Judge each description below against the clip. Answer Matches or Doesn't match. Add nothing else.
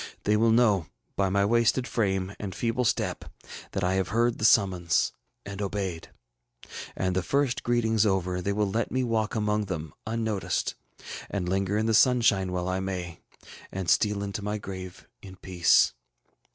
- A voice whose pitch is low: Matches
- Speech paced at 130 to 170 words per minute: Matches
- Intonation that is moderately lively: Matches